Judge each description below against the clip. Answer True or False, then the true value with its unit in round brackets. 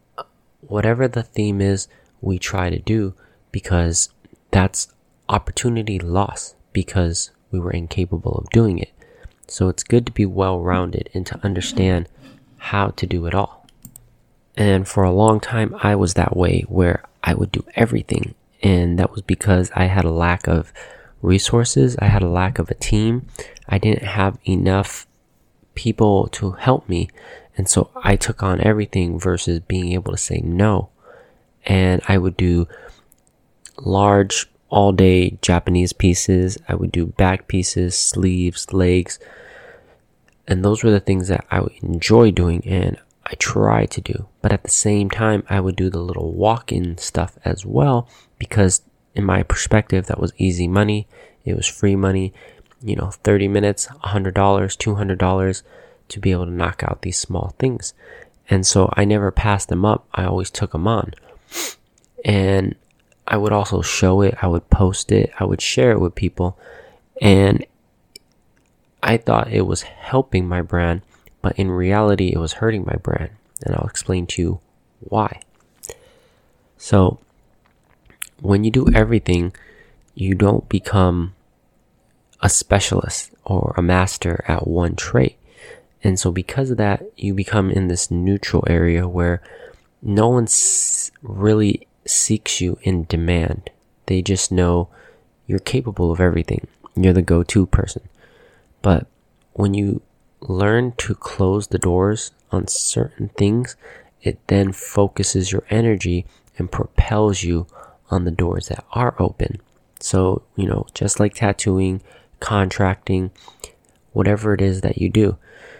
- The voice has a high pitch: False (95 Hz)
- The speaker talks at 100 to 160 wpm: True (150 wpm)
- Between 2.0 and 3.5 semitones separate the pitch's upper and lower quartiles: True (2.8 semitones)